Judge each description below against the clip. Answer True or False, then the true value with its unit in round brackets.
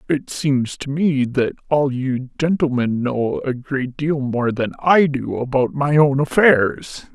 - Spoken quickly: False (170 wpm)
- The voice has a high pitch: False (135 Hz)